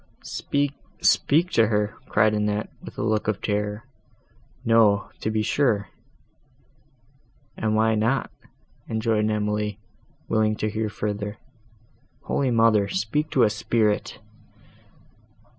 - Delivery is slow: Yes, slow, 110 wpm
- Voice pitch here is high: No, low, 110 Hz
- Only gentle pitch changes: Yes, narrow, 1.4 semitones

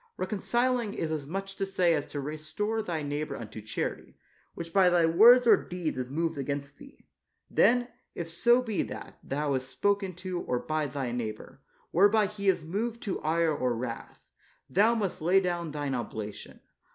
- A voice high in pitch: No, medium, 170 Hz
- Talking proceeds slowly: No, average, 175 wpm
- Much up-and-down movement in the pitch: Yes, wide, 5.7 semitones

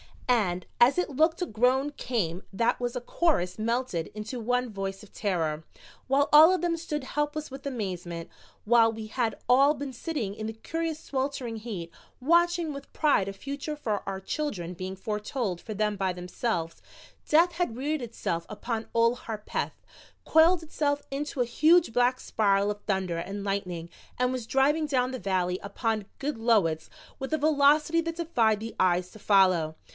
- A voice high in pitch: Yes, high, 235 Hz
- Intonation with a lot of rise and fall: Yes, wide, 6.5 semitones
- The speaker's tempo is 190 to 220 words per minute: No, average, 170 wpm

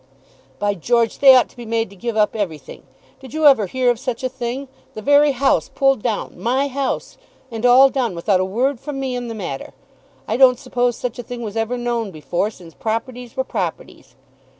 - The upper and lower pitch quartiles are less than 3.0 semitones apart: No, average, 3.3 semitones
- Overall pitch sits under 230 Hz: No, high, 240 Hz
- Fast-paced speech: Yes, fast, 210 wpm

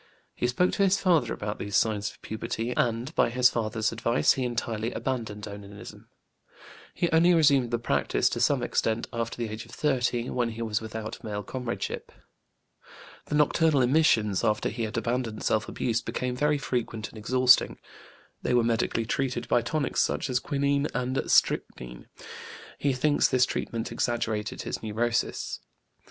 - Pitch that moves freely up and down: No, average, 2.8 semitones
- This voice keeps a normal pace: Yes, average, 160 wpm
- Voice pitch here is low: Yes, low, 120 Hz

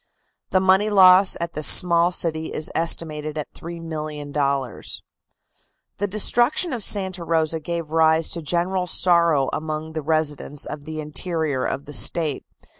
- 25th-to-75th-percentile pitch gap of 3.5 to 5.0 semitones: No, average, 2.8 semitones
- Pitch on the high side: No, medium, 160 Hz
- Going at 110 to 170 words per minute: Yes, average, 140 wpm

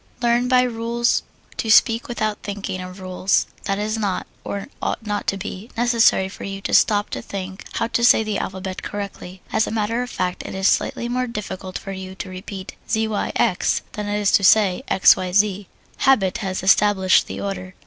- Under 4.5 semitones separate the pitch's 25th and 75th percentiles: Yes, average, 3.0 semitones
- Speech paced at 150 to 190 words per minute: No, average, 200 wpm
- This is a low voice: No, high, 205 Hz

